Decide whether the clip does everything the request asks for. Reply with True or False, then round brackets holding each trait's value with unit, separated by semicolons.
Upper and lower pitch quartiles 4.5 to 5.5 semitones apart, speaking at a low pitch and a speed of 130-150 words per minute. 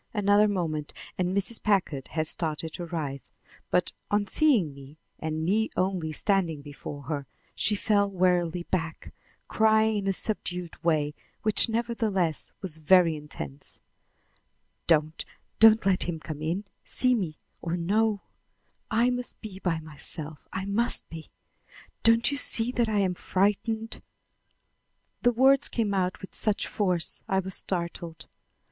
False (5.0 semitones; 185 Hz; 140 wpm)